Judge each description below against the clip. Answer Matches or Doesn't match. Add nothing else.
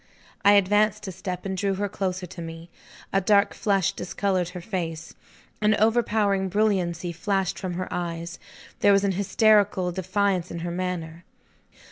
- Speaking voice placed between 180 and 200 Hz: Matches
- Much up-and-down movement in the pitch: Doesn't match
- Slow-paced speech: Doesn't match